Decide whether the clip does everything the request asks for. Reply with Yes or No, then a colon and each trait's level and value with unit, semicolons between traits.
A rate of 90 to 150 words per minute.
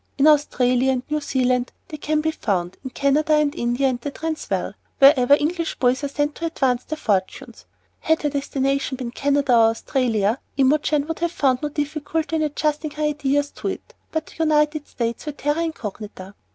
No: average, 190 wpm